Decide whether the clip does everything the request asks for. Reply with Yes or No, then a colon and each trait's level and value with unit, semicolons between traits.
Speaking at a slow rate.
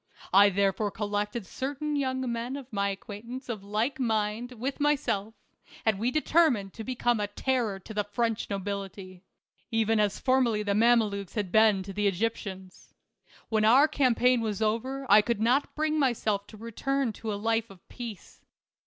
No: average, 170 wpm